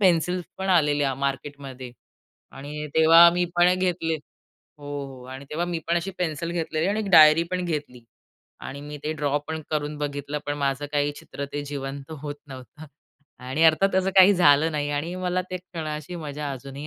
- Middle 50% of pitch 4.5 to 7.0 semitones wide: No, average, 3.2 semitones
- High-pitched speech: No, medium, 150 Hz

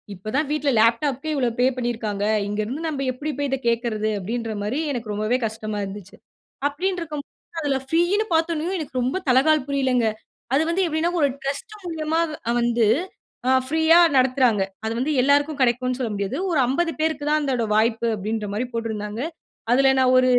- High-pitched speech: Yes, very high, 260 Hz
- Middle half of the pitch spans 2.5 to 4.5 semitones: No, average, 5.2 semitones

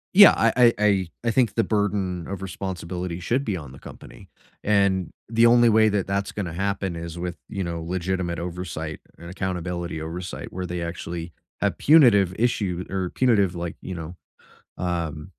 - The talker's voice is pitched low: Yes, very low, 95 Hz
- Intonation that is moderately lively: Yes, average, 3.1 semitones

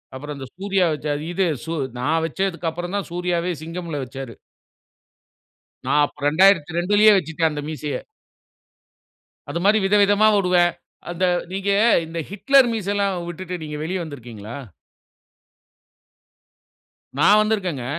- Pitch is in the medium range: Yes, medium, 175 Hz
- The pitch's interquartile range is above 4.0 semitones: Yes, average, 4.6 semitones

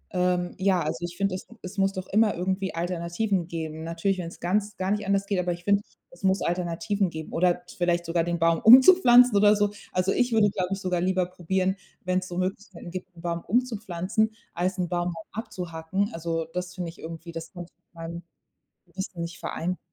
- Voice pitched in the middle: Yes, medium, 180 Hz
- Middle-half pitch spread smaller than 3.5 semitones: Yes, narrow, 2.4 semitones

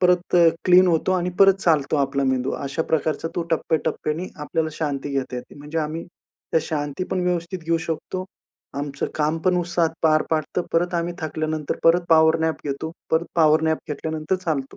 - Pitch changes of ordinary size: No, narrow, 2.3 semitones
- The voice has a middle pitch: Yes, medium, 160 Hz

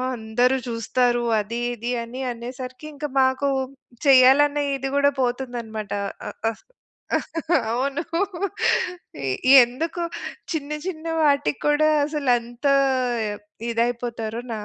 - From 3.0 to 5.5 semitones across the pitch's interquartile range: Yes, average, 3.3 semitones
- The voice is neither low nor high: No, very high, 250 Hz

